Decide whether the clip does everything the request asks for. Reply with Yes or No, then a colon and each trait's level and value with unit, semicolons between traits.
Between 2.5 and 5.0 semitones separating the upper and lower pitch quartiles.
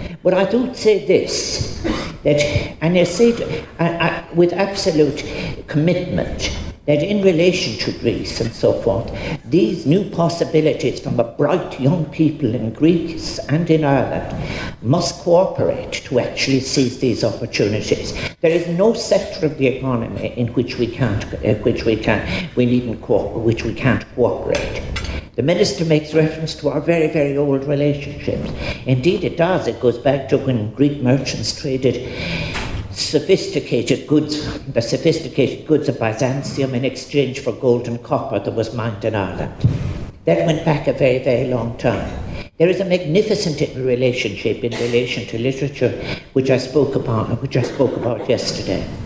No: wide, 5.4 semitones